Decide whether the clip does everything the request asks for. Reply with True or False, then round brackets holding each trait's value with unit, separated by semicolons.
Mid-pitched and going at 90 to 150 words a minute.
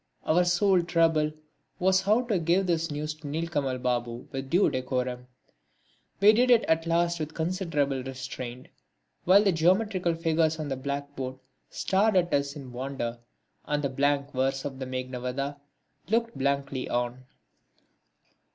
True (145 Hz; 145 wpm)